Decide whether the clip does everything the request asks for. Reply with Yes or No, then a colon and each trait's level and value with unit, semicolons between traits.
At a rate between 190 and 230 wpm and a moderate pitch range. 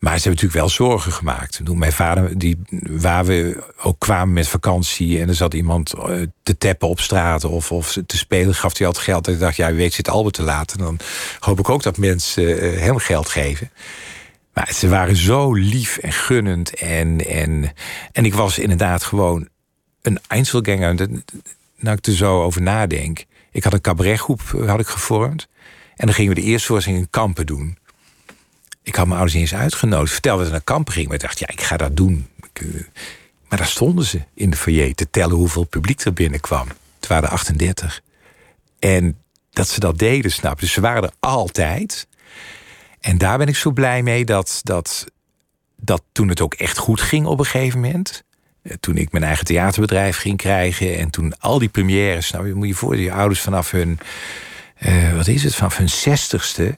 Yes: fast, 200 wpm; average, 4.0 semitones